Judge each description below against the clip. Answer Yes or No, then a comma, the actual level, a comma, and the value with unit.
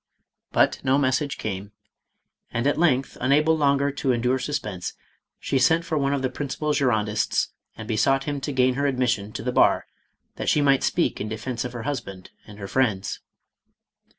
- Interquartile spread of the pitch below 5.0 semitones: Yes, average, 4.1 semitones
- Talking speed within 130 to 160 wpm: No, average, 180 wpm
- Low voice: Yes, low, 130 Hz